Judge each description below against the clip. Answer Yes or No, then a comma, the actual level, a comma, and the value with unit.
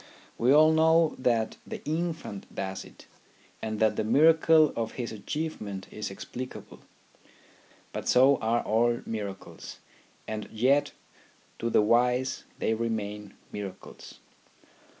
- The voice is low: Yes, low, 115 Hz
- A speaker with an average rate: No, slow, 125 wpm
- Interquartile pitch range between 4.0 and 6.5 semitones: Yes, average, 5.2 semitones